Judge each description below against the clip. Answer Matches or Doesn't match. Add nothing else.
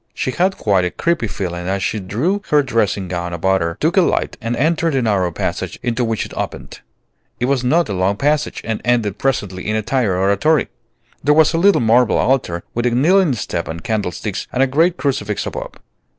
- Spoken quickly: Matches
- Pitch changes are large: Matches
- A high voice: Doesn't match